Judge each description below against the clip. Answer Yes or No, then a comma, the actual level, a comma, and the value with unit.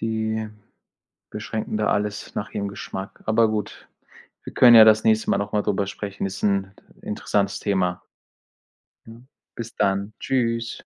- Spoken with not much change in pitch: Yes, narrow, 1.8 semitones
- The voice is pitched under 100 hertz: No, low, 105 Hz